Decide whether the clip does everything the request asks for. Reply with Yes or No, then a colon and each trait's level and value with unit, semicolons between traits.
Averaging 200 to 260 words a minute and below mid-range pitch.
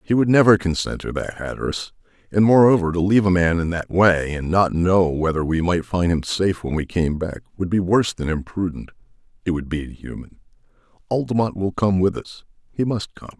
Yes: fast, 205 wpm; very low, 90 Hz